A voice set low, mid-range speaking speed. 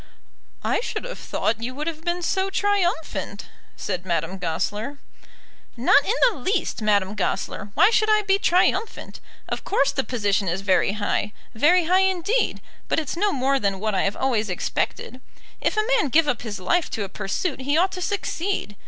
No: very high, 275 Hz; average, 185 wpm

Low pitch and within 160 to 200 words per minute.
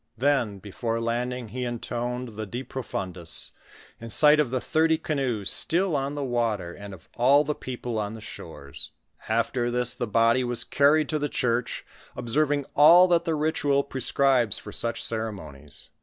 Yes: low, 125 Hz; average, 170 wpm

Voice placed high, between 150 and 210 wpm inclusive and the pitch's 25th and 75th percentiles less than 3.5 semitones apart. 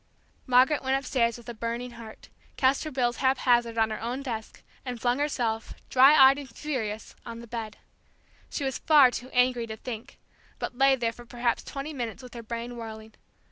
Yes: high, 245 Hz; average, 190 wpm; narrow, 2.4 semitones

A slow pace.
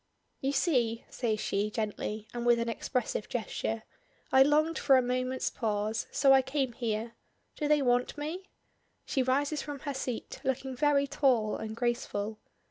No: average, 160 wpm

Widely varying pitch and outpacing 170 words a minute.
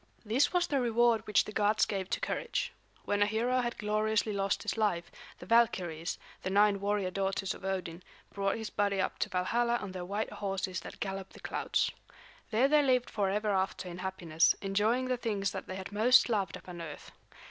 No: average, 2.9 semitones; average, 195 wpm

